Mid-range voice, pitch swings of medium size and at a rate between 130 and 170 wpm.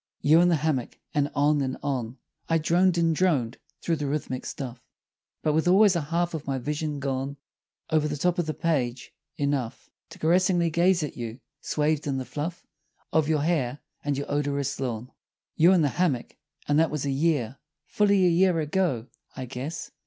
No: medium, 150 Hz; average, 3.7 semitones; average, 190 wpm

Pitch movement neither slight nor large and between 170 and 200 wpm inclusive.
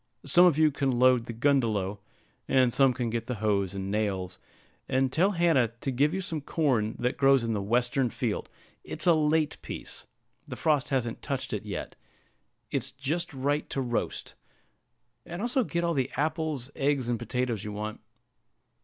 Yes: average, 4.6 semitones; average, 175 wpm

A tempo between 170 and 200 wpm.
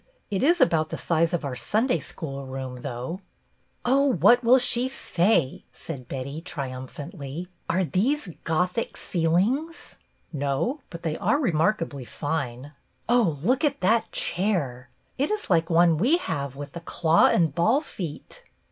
No: average, 160 wpm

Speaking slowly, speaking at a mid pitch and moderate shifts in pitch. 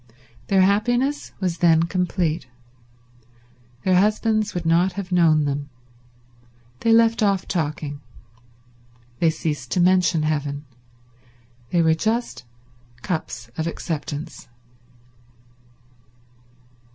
Yes: slow, 95 wpm; medium, 175 Hz; average, 4.2 semitones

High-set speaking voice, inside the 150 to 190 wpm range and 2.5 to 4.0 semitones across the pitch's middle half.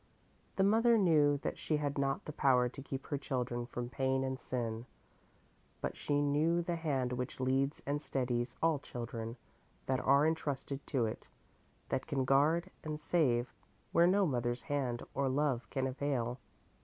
No: low, 135 Hz; average, 165 wpm; average, 3.0 semitones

